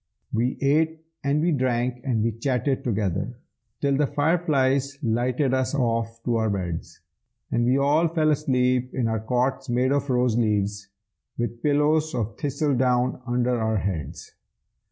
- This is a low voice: Yes, low, 125 Hz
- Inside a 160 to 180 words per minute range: No, average, 150 wpm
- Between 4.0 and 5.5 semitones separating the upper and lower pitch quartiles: No, average, 3.5 semitones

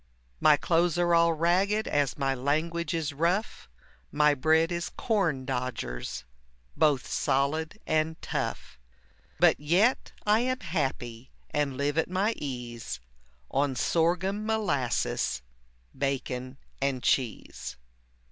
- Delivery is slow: Yes, slow, 115 wpm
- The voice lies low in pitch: No, medium, 150 Hz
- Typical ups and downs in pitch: Yes, average, 4.5 semitones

